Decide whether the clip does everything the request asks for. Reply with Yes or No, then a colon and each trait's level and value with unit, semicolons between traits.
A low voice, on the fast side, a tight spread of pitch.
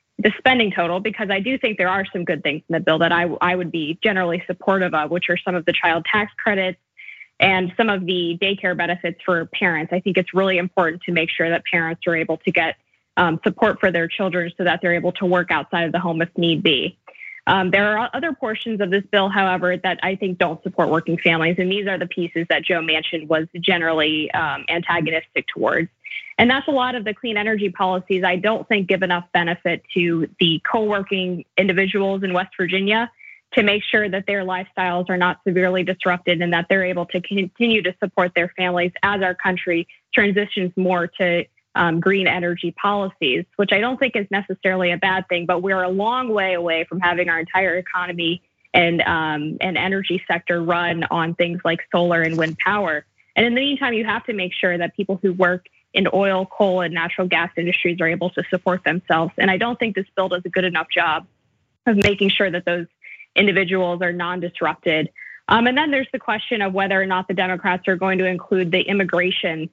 No: medium, 185 Hz; fast, 215 wpm; narrow, 2.2 semitones